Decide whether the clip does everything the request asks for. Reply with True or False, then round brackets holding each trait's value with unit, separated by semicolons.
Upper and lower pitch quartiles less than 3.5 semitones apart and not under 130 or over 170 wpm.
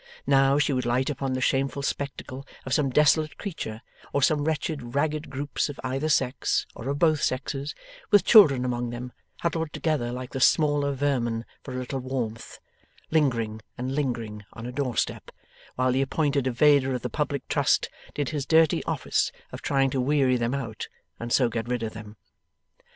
False (2.8 semitones; 180 wpm)